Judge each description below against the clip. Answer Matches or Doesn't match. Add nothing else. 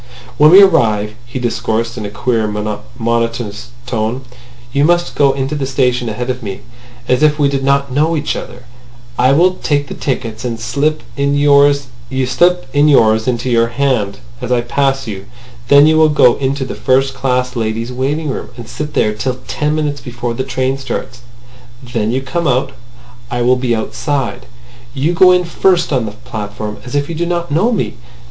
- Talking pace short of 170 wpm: Doesn't match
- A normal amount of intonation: Matches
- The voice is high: Doesn't match